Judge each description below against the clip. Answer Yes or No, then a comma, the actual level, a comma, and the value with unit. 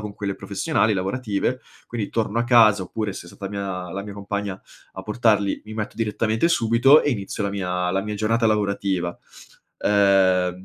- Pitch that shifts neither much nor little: No, narrow, 2.3 semitones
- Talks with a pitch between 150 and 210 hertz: No, low, 100 Hz